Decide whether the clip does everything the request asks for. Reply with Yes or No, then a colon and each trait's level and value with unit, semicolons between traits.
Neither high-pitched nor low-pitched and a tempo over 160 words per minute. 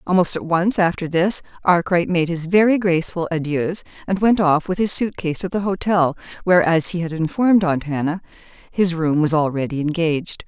Yes: medium, 170 Hz; average, 190 wpm